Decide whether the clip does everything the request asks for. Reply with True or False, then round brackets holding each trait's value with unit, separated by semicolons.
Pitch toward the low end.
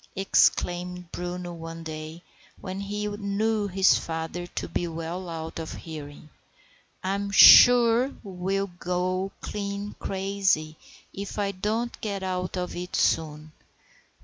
False (185 Hz)